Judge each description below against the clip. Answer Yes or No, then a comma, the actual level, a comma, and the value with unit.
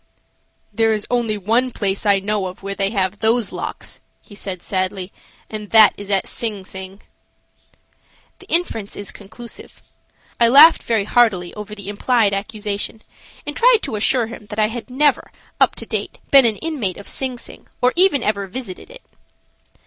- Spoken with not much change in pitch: No, average, 3.4 semitones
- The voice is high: Yes, high, 215 Hz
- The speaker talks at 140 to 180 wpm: Yes, average, 170 wpm